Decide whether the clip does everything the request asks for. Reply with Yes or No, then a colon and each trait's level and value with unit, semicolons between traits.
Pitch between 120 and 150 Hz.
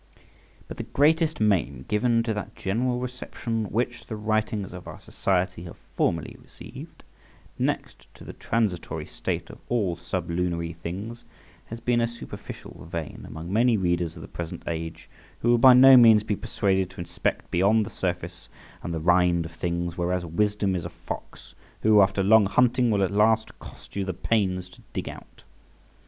No: low, 100 Hz